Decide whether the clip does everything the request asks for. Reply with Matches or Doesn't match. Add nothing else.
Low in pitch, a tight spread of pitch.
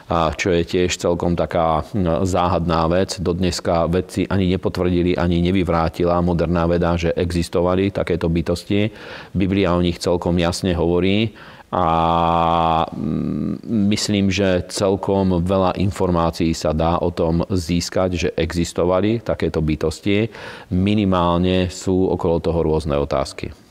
Matches